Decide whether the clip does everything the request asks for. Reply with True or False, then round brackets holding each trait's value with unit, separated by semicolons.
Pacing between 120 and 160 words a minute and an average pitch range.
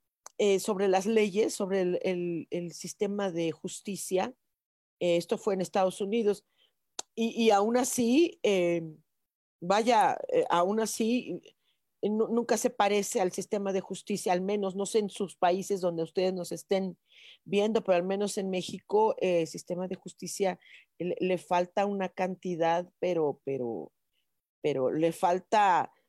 True (150 wpm; 3.0 semitones)